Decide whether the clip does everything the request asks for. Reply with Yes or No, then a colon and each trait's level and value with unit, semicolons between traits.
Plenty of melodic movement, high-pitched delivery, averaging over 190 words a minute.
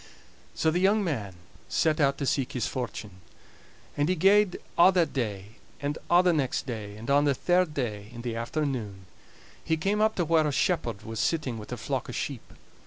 No: wide, 6.8 semitones; medium, 140 Hz; average, 200 wpm